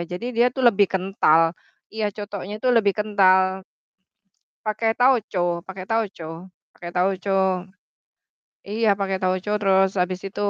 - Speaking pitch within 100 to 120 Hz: No, high, 195 Hz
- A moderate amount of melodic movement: No, narrow, 2.2 semitones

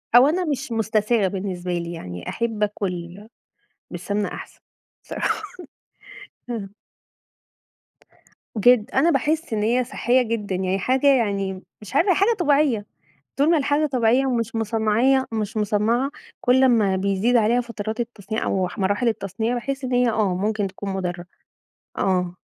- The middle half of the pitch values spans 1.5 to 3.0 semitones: No, average, 4.1 semitones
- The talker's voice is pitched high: Yes, high, 220 Hz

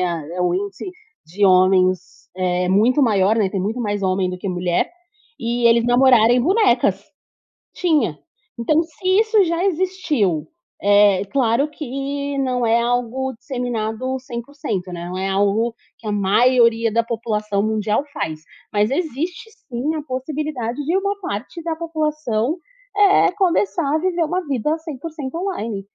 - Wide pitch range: Yes, wide, 7.0 semitones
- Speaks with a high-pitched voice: Yes, high, 240 Hz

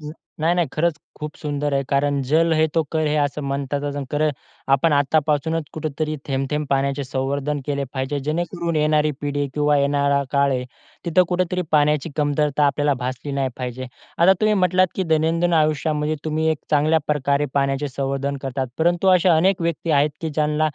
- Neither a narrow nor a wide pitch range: No, narrow, 2.2 semitones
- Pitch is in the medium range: Yes, medium, 150 Hz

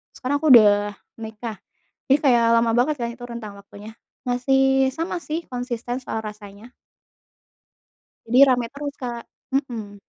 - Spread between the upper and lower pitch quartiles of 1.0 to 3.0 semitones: No, average, 3.4 semitones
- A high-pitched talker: Yes, high, 240 Hz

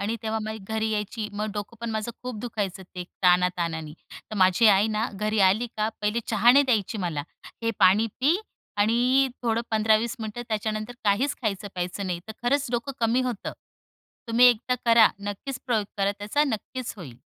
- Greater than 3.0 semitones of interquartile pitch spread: No, average, 2.7 semitones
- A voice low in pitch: No, high, 220 Hz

